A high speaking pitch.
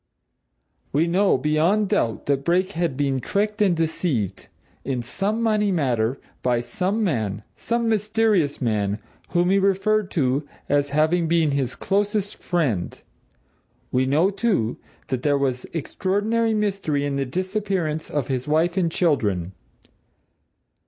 No: medium, 160 Hz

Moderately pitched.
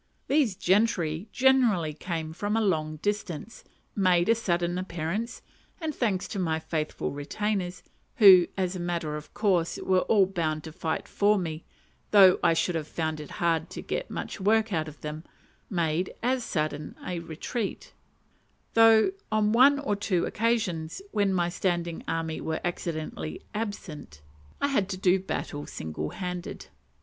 Yes: medium, 180 Hz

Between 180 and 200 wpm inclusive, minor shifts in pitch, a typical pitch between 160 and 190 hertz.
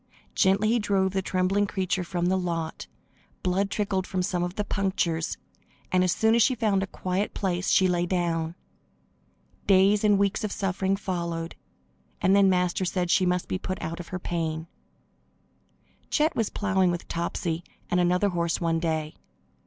No: average, 170 wpm; narrow, 2.1 semitones; medium, 185 Hz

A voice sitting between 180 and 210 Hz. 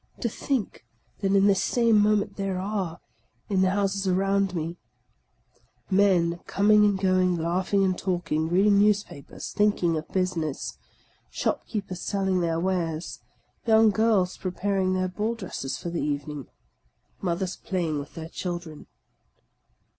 Yes: medium, 185 Hz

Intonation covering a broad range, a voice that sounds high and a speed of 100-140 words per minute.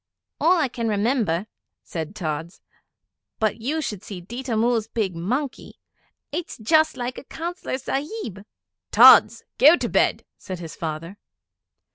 Yes: wide, 6.9 semitones; high, 225 Hz; slow, 135 wpm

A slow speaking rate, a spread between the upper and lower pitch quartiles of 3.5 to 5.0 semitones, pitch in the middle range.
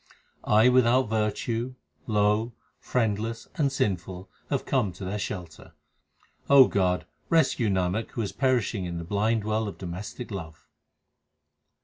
No: slow, 125 wpm; average, 4.0 semitones; low, 105 Hz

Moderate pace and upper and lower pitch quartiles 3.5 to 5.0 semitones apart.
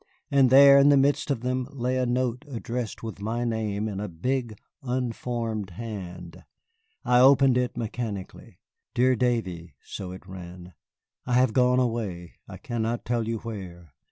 Yes: average, 155 wpm; average, 3.9 semitones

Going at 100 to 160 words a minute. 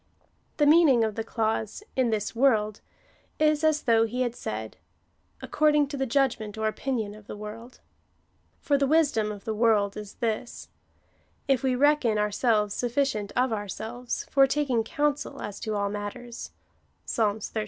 No: average, 175 wpm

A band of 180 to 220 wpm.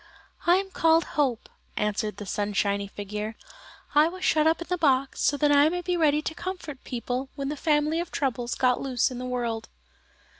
Yes: average, 195 wpm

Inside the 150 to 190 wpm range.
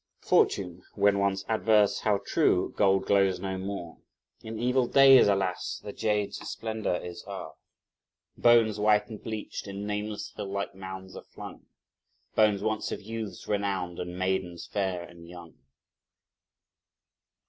No: slow, 135 wpm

